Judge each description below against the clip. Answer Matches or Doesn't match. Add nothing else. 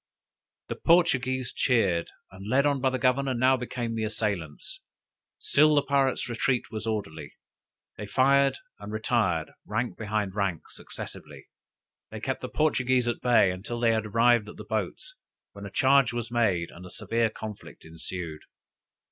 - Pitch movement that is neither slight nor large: Matches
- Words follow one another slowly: Doesn't match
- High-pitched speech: Doesn't match